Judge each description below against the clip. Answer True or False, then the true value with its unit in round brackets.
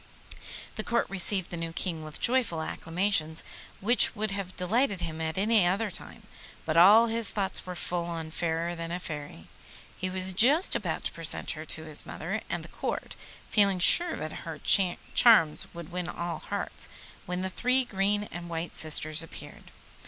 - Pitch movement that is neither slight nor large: True (3.9 semitones)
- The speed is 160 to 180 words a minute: True (175 wpm)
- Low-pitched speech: False (180 Hz)